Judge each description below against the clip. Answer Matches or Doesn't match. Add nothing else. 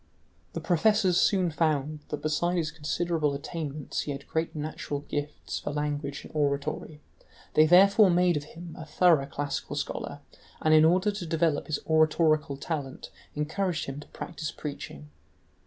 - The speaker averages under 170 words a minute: Matches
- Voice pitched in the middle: Matches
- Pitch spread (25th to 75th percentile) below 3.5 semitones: Matches